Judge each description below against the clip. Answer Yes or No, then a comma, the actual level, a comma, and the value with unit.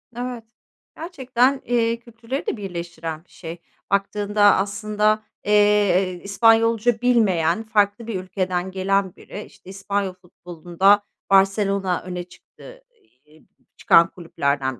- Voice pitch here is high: Yes, high, 200 Hz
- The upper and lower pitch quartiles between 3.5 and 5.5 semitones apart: Yes, average, 3.9 semitones